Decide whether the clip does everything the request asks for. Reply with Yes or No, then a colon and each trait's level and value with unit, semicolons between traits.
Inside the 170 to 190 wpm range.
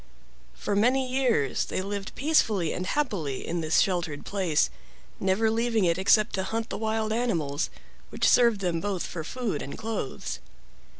No: average, 160 wpm